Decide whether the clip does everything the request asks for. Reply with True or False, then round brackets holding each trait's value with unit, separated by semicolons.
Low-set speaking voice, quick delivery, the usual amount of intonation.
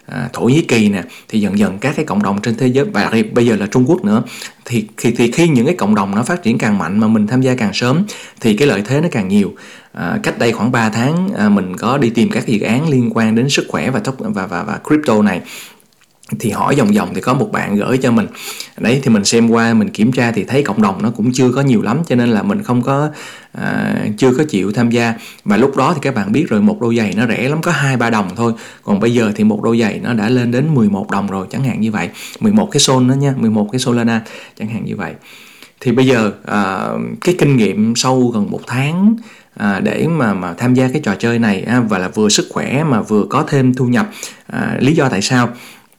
False (130 Hz; 265 wpm; 8.2 semitones)